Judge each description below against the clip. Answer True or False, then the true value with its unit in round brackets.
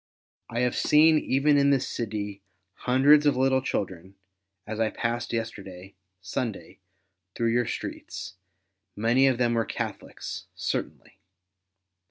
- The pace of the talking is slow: True (125 wpm)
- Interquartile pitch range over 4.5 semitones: False (3.9 semitones)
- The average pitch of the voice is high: False (120 Hz)